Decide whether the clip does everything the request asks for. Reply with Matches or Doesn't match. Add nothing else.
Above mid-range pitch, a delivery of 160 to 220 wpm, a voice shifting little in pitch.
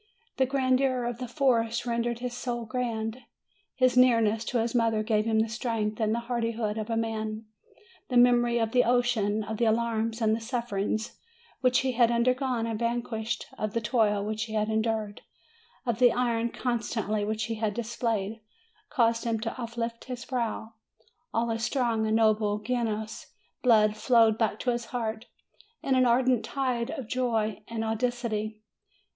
Matches